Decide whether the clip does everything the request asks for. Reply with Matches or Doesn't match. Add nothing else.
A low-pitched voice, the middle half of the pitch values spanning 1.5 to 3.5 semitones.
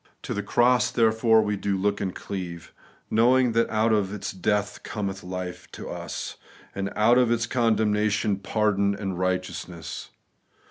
Matches